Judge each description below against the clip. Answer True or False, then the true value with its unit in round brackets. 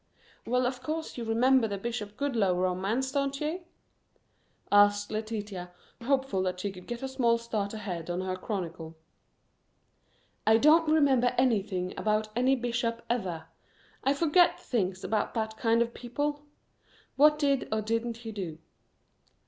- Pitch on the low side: False (230 Hz)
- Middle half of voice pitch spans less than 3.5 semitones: False (4.6 semitones)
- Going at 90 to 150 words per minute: True (145 wpm)